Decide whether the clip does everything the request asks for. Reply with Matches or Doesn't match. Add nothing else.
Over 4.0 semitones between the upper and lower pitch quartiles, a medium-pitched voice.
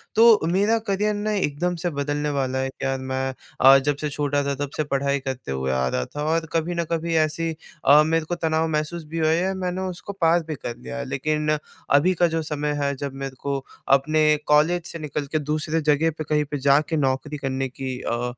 Doesn't match